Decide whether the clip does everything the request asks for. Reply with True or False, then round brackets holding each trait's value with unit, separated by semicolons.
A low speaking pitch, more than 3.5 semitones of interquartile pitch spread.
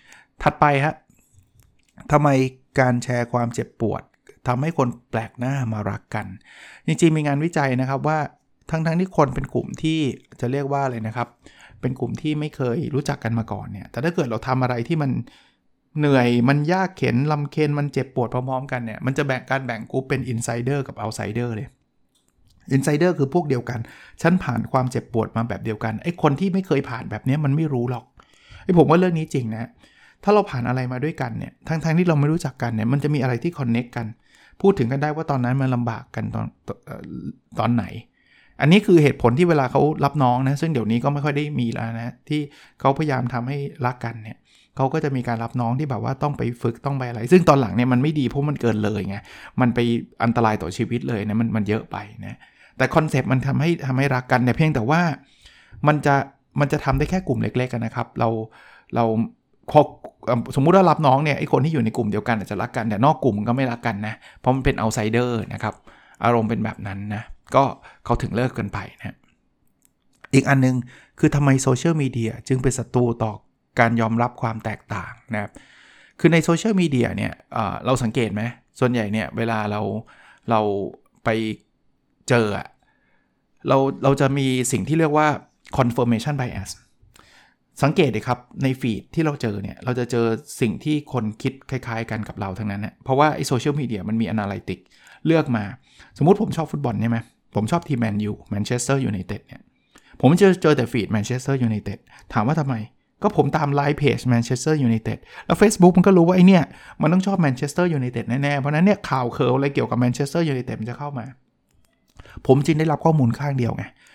True (130 Hz; 4.2 semitones)